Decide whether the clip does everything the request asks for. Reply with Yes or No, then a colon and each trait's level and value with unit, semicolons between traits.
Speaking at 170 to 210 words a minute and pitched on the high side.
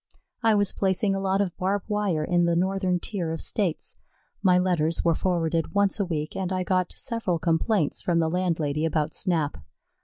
No: average, 185 wpm; medium, 180 Hz